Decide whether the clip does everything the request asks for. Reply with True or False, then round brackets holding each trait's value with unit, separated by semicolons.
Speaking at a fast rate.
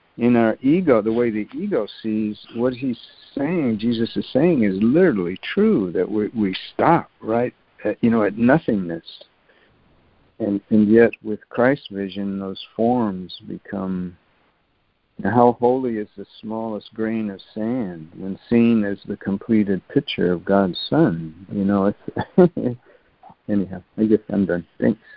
False (150 wpm)